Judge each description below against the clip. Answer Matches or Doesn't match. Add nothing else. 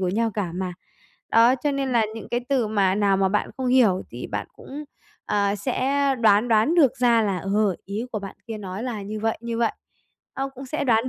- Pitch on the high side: Matches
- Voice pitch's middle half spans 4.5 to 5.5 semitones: Doesn't match